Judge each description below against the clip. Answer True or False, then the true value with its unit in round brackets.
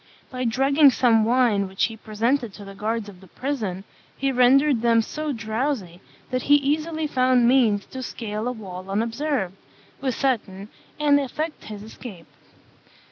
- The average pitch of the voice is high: True (235 Hz)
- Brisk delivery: False (155 wpm)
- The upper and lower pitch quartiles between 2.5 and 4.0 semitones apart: False (4.6 semitones)